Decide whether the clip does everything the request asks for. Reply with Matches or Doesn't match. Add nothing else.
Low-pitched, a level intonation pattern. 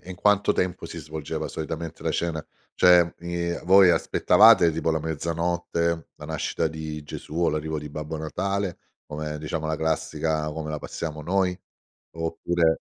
Matches